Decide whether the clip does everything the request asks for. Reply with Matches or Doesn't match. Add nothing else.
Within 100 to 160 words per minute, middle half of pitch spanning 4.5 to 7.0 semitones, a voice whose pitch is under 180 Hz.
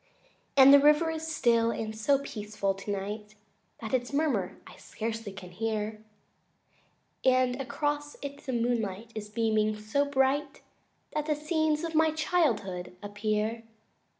Doesn't match